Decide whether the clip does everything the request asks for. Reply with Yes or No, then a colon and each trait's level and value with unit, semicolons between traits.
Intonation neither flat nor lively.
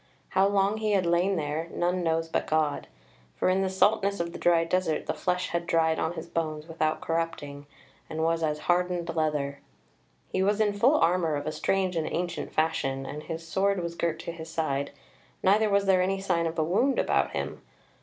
Yes: average, 3.0 semitones